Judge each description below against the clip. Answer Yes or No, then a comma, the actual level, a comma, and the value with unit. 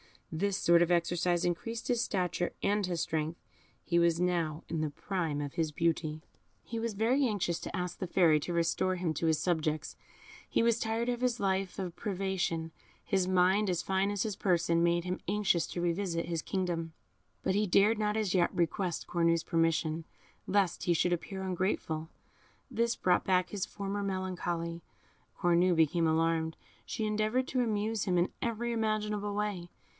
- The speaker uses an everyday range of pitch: Yes, average, 3.5 semitones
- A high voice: No, medium, 180 Hz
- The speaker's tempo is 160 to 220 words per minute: Yes, average, 175 wpm